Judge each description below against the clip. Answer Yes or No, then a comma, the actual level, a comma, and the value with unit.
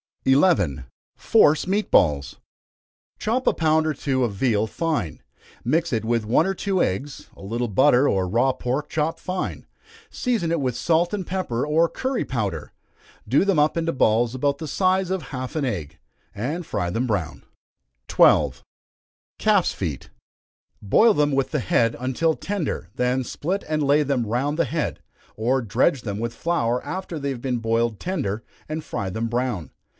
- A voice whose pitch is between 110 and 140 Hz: Yes, low, 135 Hz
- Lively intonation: Yes, wide, 6.1 semitones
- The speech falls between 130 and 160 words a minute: No, average, 170 wpm